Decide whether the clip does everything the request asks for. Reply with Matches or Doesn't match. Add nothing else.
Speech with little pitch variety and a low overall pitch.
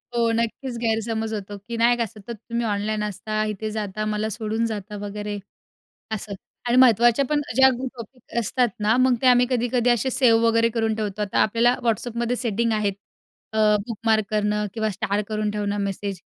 Doesn't match